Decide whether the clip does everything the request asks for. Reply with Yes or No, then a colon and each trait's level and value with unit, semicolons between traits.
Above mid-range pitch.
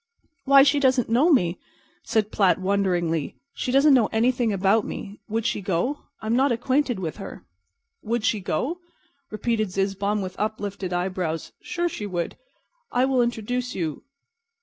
Yes: high, 215 Hz